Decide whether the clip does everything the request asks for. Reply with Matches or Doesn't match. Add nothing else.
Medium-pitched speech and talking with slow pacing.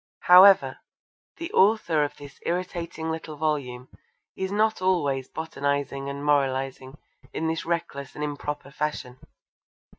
Matches